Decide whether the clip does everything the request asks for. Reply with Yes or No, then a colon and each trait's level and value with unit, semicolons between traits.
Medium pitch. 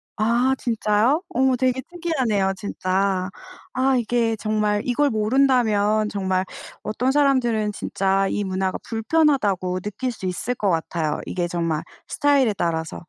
No: high, 215 Hz